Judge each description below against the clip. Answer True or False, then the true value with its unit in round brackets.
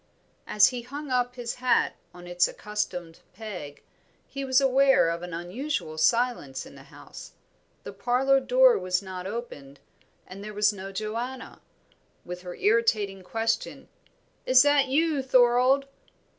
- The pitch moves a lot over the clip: True (5.8 semitones)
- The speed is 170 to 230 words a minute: False (145 wpm)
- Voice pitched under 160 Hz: False (230 Hz)